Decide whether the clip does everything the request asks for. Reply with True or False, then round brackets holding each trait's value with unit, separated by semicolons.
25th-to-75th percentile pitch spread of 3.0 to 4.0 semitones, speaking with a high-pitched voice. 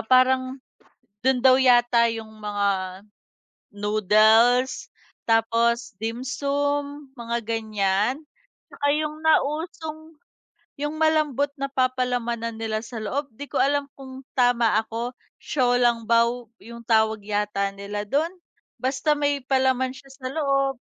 True (3.7 semitones; 245 Hz)